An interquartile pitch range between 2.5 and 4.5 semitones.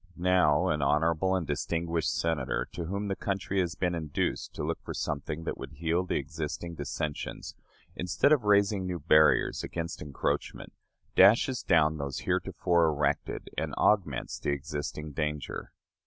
Yes: average, 3.5 semitones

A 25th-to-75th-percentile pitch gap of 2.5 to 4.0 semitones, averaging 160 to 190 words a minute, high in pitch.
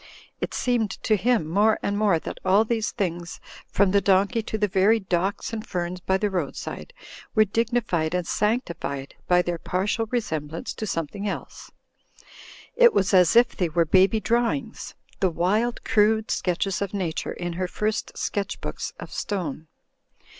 Yes: average, 3.7 semitones; average, 165 wpm; high, 200 Hz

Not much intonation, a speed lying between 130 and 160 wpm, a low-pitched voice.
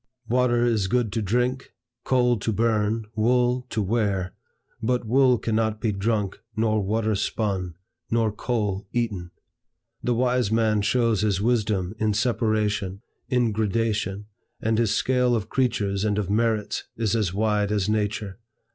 Yes: narrow, 2.3 semitones; average, 145 wpm; low, 110 Hz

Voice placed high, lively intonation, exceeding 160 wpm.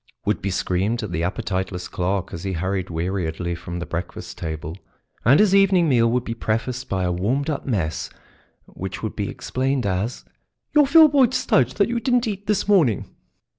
No: low, 105 Hz; wide, 8.4 semitones; average, 180 wpm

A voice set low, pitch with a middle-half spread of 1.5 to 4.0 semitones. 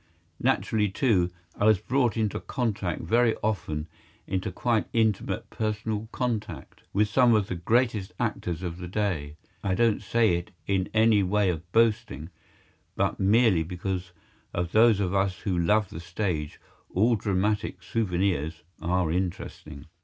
Yes: low, 100 Hz; average, 3.7 semitones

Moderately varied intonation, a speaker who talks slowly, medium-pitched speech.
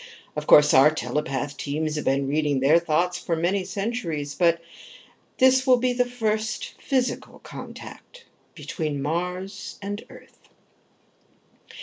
No: wide, 6.4 semitones; slow, 125 wpm; medium, 170 Hz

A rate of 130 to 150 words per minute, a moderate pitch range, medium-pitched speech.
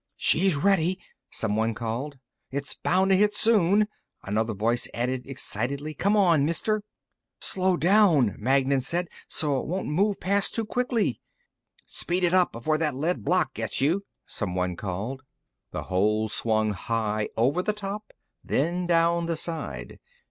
No: average, 145 wpm; wide, 8.3 semitones; medium, 155 Hz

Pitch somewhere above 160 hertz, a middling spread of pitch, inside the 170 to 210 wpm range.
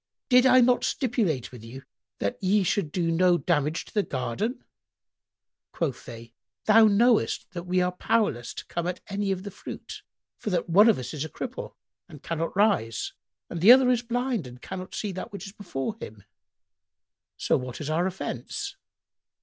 No: medium, 185 Hz; wide, 6.4 semitones; average, 180 wpm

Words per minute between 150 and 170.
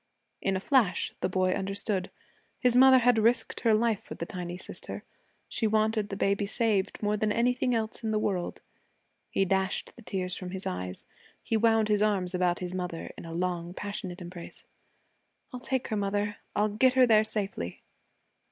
No: average, 180 wpm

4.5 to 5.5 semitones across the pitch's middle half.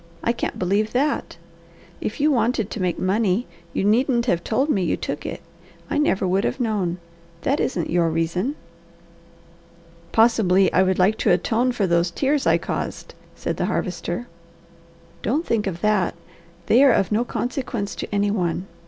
Yes: average, 4.8 semitones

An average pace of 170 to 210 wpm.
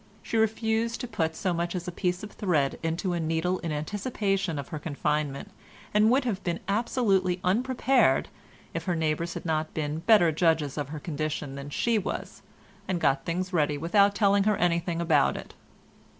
Yes: average, 180 wpm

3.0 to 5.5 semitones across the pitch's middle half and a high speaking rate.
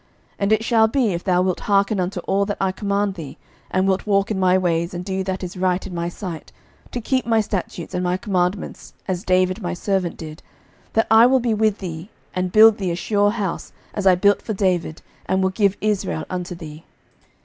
No: narrow, 2.5 semitones; fast, 220 wpm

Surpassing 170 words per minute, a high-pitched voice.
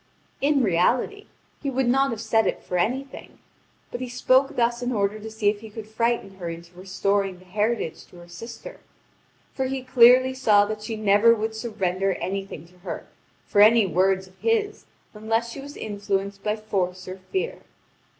Yes: average, 180 wpm; high, 215 Hz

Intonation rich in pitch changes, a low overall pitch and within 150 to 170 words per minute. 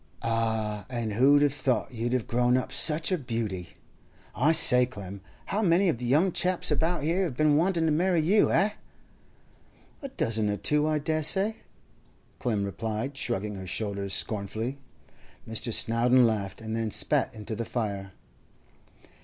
Yes: wide, 6.1 semitones; low, 125 Hz; average, 160 wpm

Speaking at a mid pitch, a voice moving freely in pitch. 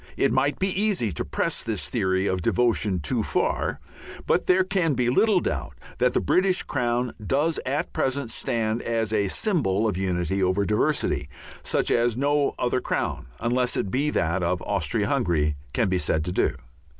No: low, 115 Hz; wide, 6.9 semitones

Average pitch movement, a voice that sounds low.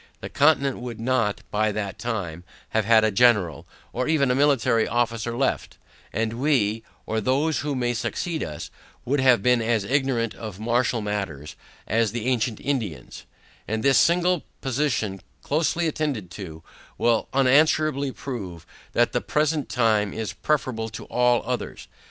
Yes: average, 4.0 semitones; low, 120 Hz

